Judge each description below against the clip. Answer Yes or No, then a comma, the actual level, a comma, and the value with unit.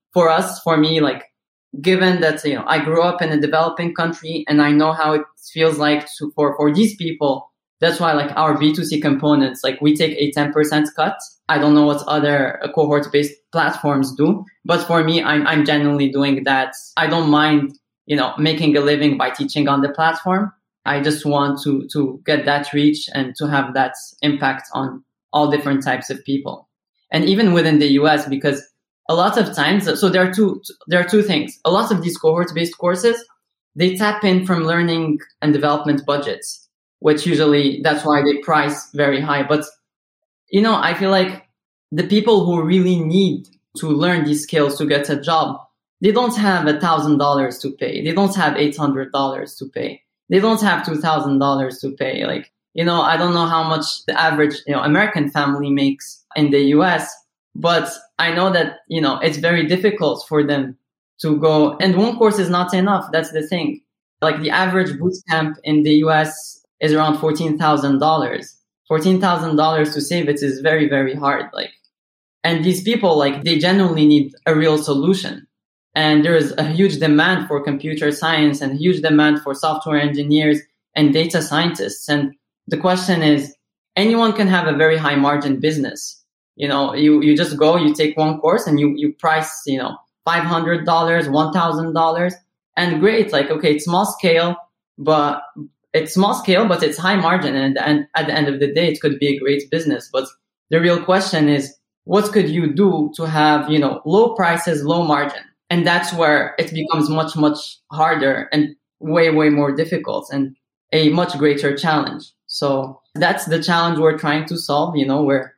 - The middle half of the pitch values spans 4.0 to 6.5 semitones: No, narrow, 2.6 semitones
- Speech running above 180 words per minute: Yes, average, 190 wpm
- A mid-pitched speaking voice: Yes, medium, 155 Hz